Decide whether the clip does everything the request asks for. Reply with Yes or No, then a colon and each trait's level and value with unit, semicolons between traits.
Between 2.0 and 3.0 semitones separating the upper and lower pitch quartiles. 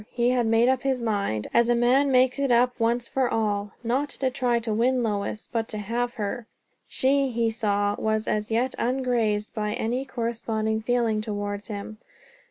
Yes: narrow, 2.6 semitones